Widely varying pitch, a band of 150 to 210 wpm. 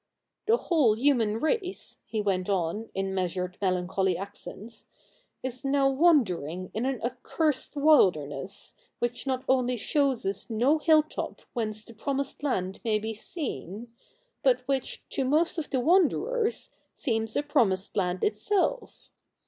No: wide, 6.6 semitones; slow, 135 wpm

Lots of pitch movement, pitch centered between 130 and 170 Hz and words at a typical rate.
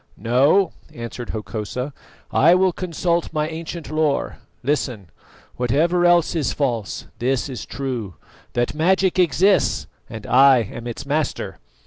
No: wide, 5.8 semitones; medium, 140 Hz; slow, 125 wpm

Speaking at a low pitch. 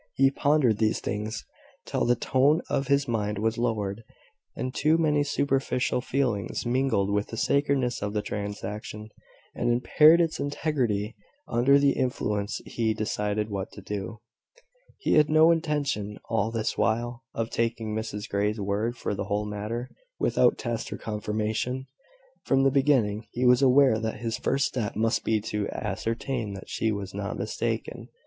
Yes: low, 115 Hz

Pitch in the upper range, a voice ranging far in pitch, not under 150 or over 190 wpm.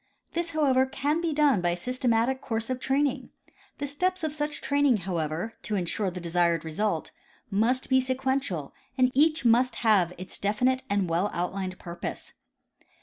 Yes: high, 240 Hz; wide, 6.8 semitones; average, 165 wpm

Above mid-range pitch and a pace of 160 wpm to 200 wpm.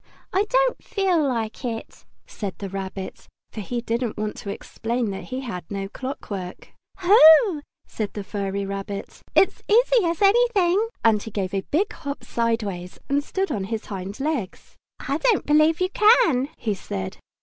Yes: high, 240 Hz; average, 170 wpm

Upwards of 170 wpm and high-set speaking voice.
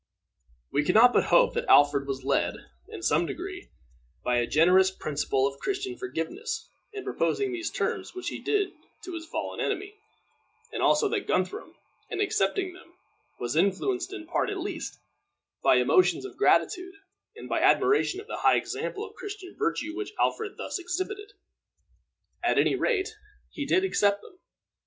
No: average, 165 wpm; very high, 365 Hz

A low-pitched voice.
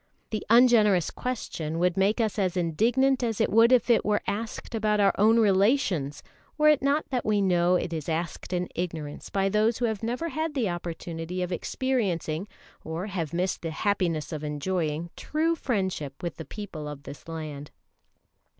No: high, 190 Hz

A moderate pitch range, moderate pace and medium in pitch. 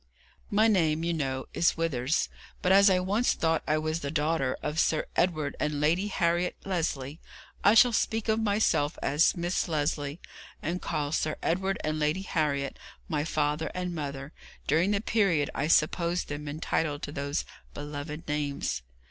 Yes: average, 3.5 semitones; average, 165 wpm; medium, 155 Hz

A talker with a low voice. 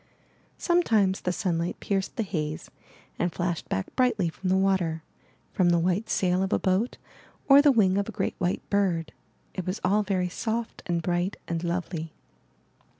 No: medium, 185 Hz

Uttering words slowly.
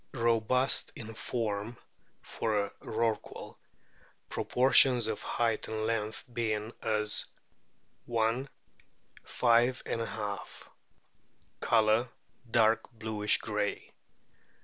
Yes: slow, 80 wpm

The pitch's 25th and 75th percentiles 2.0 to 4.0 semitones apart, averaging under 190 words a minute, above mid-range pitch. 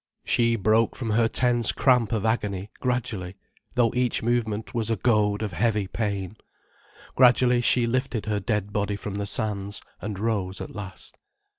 No: narrow, 2.6 semitones; average, 160 wpm; low, 110 Hz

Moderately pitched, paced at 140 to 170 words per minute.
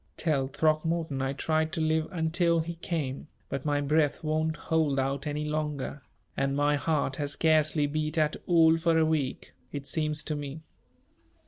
Yes: medium, 155 Hz; average, 165 wpm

